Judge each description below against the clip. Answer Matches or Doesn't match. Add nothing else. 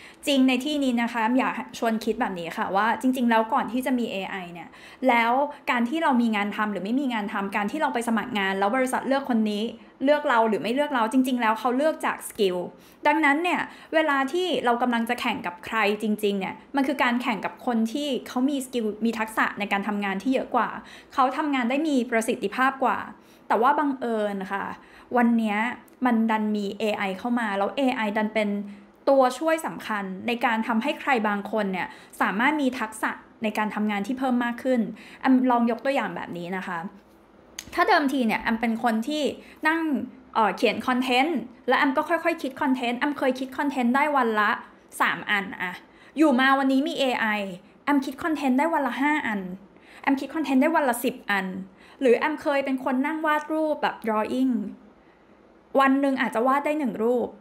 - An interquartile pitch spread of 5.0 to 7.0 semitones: Doesn't match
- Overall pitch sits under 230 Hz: Doesn't match